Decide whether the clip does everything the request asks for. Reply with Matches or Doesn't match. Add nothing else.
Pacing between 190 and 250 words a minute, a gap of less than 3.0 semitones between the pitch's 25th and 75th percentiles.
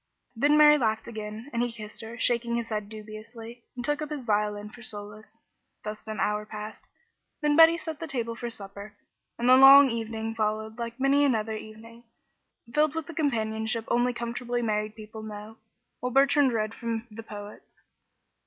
Doesn't match